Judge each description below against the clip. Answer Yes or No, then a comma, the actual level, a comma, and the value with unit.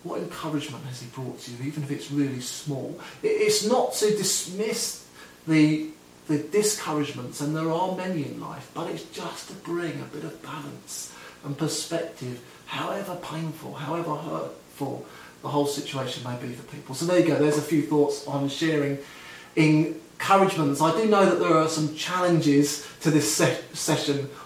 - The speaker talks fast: No, average, 170 wpm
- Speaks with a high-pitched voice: No, medium, 150 Hz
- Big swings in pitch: No, average, 2.7 semitones